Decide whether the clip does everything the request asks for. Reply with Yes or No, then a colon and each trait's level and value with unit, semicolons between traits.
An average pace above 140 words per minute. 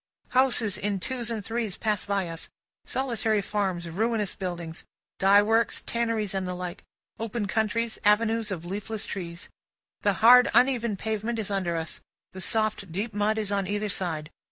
Yes: average, 160 wpm